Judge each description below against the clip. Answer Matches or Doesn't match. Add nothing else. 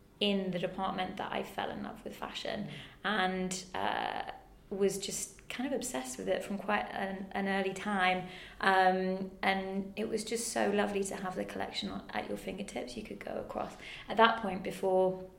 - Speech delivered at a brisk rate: Doesn't match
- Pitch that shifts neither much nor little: Doesn't match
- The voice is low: Doesn't match